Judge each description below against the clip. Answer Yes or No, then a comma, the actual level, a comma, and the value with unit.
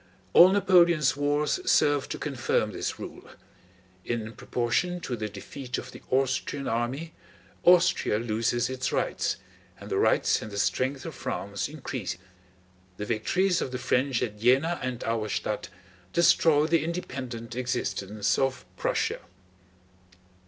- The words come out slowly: Yes, slow, 130 wpm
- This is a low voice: Yes, low, 130 Hz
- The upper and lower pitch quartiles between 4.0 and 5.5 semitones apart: Yes, average, 5.0 semitones